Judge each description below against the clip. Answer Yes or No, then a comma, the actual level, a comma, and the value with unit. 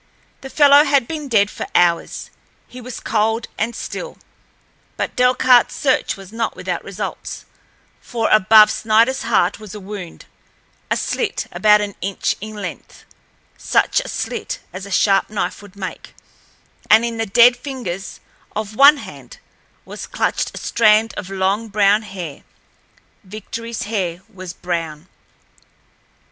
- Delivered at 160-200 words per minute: No, slow, 135 wpm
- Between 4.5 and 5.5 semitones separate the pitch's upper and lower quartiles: No, average, 3.3 semitones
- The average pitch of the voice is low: No, high, 215 Hz